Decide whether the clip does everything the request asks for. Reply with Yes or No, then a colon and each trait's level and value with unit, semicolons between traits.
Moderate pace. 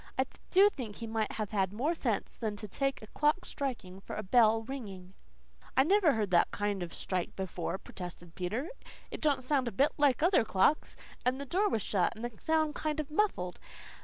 No: fast, 210 wpm